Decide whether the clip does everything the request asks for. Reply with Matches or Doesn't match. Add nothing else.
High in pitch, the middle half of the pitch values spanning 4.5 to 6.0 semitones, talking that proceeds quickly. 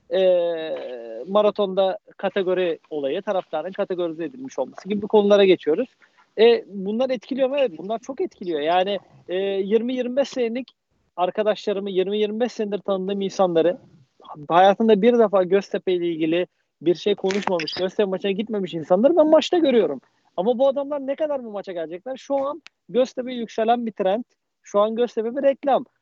Matches